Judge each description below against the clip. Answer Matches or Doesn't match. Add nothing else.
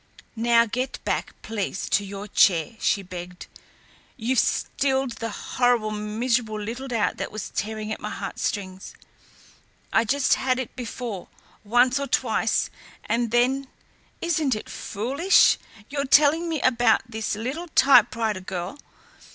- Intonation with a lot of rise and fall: Doesn't match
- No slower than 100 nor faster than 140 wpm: Matches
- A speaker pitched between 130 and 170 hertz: Doesn't match